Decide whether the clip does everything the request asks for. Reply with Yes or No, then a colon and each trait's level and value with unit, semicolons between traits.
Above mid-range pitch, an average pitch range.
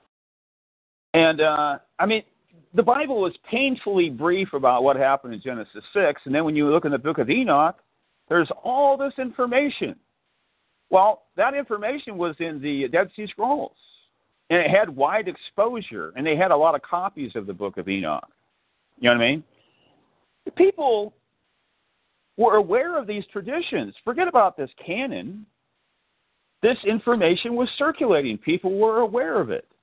No: high, 210 Hz; wide, 9.0 semitones